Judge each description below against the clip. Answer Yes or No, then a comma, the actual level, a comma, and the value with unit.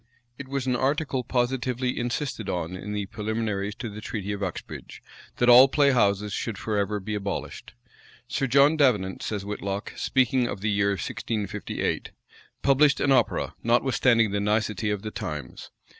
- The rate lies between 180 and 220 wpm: No, average, 160 wpm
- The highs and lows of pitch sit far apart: No, average, 4.1 semitones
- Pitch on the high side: No, low, 110 Hz